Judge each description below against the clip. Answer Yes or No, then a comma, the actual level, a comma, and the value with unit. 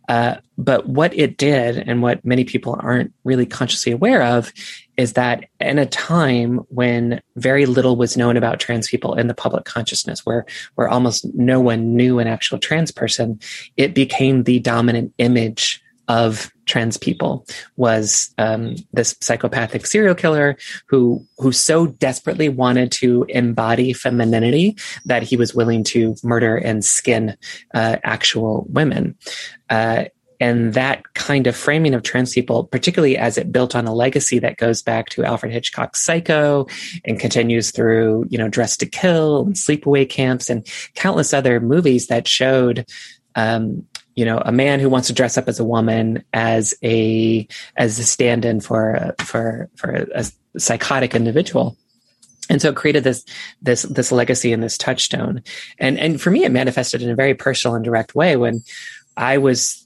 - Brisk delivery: No, average, 165 wpm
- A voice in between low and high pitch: No, low, 120 Hz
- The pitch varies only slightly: Yes, narrow, 2.3 semitones